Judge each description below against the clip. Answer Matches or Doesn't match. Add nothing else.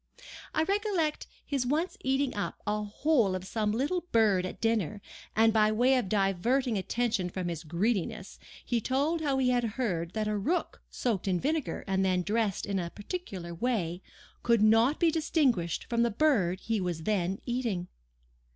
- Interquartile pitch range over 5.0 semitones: Matches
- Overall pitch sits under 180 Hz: Doesn't match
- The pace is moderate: Matches